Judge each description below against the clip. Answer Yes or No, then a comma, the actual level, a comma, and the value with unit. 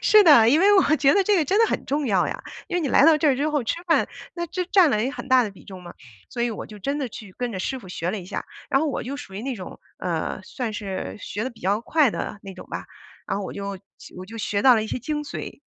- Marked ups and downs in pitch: Yes, wide, 6.9 semitones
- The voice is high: Yes, very high, 255 Hz